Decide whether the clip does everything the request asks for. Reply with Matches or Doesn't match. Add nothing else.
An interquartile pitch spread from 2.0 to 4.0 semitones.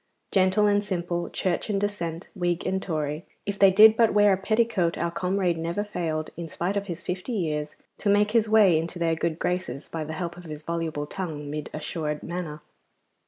Matches